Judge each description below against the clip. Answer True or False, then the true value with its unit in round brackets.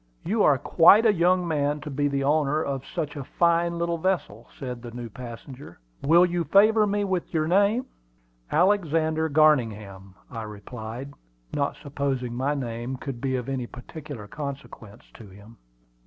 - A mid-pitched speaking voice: True (145 Hz)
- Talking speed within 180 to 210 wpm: False (160 wpm)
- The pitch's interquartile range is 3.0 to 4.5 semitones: False (5.6 semitones)